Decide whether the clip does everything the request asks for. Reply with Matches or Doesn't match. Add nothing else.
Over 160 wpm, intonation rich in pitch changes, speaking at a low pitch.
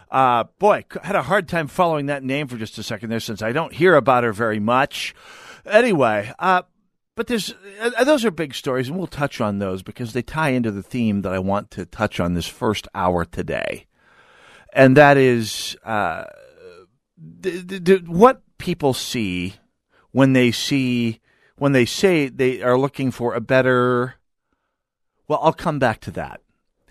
Matches